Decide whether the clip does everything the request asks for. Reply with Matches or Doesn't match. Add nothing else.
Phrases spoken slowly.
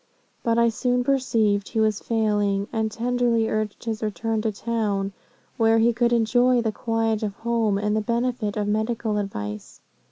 Doesn't match